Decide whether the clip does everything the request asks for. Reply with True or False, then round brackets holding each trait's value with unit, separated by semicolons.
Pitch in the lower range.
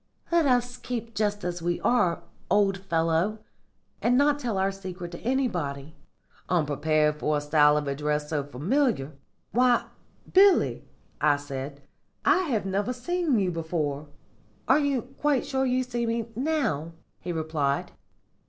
False (190 Hz)